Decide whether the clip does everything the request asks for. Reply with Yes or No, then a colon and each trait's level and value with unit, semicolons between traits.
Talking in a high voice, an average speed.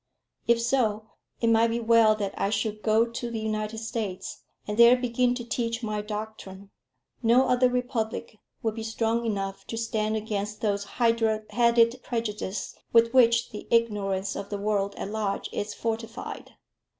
Yes: high, 225 Hz; average, 160 wpm